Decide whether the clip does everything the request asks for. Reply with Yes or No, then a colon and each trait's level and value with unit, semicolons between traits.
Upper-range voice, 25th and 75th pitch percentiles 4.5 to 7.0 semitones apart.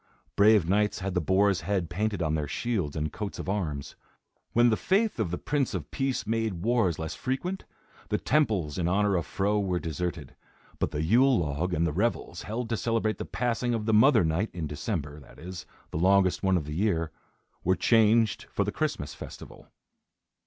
No: very low, 95 Hz; average, 5.2 semitones